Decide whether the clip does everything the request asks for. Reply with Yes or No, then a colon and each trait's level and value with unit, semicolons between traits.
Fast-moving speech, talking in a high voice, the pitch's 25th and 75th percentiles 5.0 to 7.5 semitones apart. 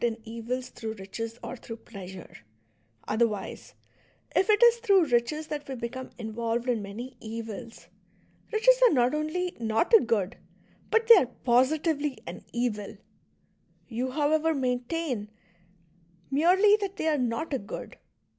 No: average, 145 wpm; very high, 250 Hz; wide, 5.6 semitones